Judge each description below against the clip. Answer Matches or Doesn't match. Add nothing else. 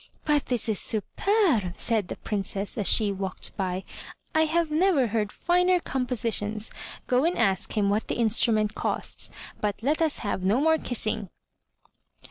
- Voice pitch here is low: Doesn't match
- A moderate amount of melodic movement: Doesn't match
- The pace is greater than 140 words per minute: Matches